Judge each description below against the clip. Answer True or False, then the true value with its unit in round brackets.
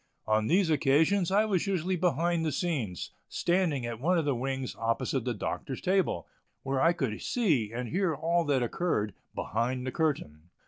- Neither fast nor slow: True (175 wpm)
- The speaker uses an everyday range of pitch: False (6.2 semitones)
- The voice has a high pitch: False (145 Hz)